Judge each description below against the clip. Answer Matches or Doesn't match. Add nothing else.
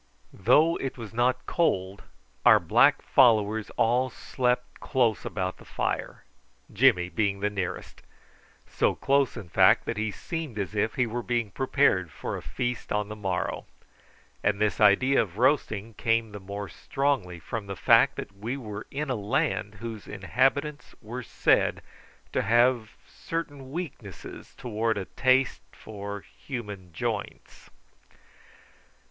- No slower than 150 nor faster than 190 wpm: Doesn't match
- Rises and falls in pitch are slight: Doesn't match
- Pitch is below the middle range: Matches